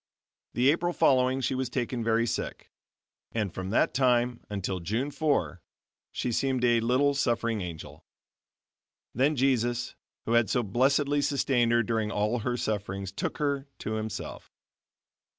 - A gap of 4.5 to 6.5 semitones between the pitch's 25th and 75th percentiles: No, average, 3.4 semitones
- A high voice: No, low, 120 Hz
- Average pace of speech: Yes, average, 145 wpm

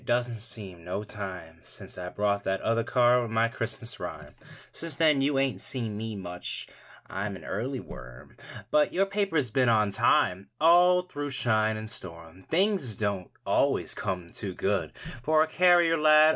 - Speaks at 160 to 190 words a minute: Yes, average, 170 wpm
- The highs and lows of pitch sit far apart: Yes, wide, 7.3 semitones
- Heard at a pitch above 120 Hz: No, low, 115 Hz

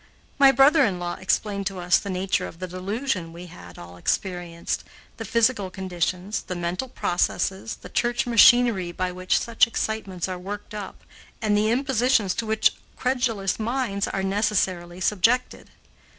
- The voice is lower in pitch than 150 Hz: No, high, 195 Hz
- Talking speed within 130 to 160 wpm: Yes, average, 155 wpm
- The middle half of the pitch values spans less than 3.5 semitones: No, average, 4.2 semitones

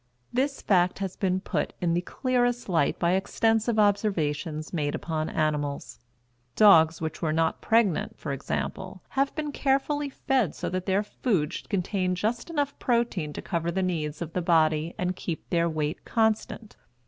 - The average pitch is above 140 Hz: Yes, medium, 185 Hz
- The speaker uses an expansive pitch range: Yes, wide, 5.8 semitones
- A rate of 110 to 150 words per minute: No, average, 165 wpm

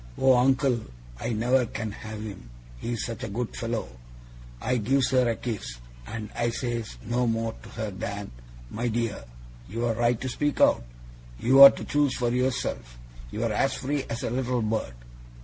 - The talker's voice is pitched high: No, low, 120 Hz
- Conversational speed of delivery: Yes, average, 170 wpm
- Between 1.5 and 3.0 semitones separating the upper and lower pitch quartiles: Yes, narrow, 2.6 semitones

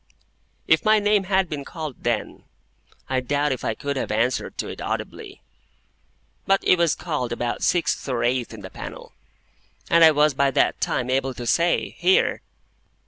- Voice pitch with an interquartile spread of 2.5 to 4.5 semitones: No, average, 5.1 semitones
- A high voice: No, medium, 140 Hz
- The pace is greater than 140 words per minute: Yes, average, 175 wpm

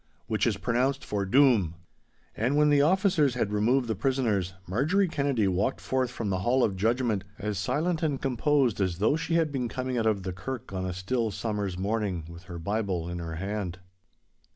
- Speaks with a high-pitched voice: No, low, 110 Hz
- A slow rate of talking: No, average, 195 wpm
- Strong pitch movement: Yes, wide, 5.7 semitones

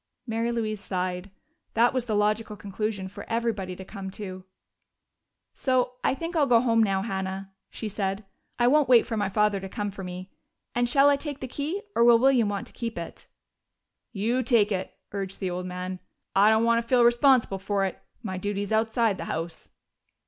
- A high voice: Yes, high, 215 Hz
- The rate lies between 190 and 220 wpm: Yes, average, 195 wpm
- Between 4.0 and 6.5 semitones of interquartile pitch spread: No, average, 3.6 semitones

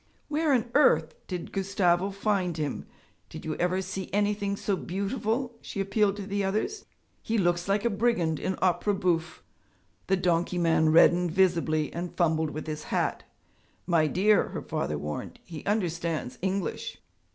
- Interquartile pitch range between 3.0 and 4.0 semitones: Yes, average, 3.3 semitones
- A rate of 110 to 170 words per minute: Yes, average, 155 wpm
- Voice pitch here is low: No, medium, 185 Hz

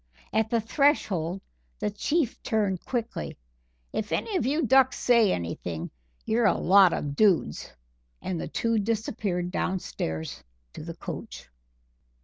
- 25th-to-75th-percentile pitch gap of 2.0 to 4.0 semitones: No, average, 4.8 semitones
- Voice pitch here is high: Yes, high, 210 Hz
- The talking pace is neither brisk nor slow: No, slow, 130 wpm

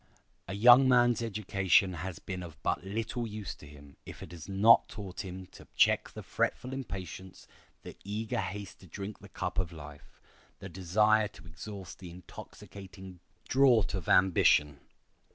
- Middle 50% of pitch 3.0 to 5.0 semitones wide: Yes, average, 3.3 semitones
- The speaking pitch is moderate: No, very low, 95 Hz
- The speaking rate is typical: Yes, average, 160 wpm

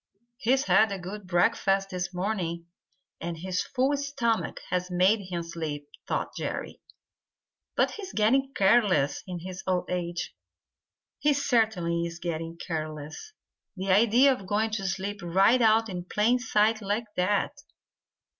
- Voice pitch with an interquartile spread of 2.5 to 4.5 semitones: Yes, average, 4.2 semitones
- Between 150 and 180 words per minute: No, average, 140 wpm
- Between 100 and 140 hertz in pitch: No, high, 195 Hz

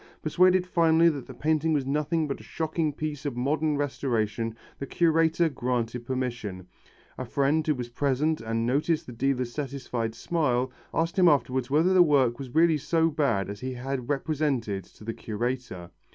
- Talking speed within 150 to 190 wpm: Yes, average, 170 wpm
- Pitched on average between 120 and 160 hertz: Yes, medium, 140 Hz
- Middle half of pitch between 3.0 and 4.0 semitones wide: No, average, 4.4 semitones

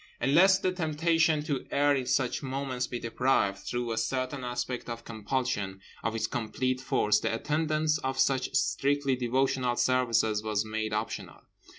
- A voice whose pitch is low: Yes, low, 130 Hz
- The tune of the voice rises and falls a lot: No, average, 3.8 semitones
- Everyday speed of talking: Yes, average, 160 wpm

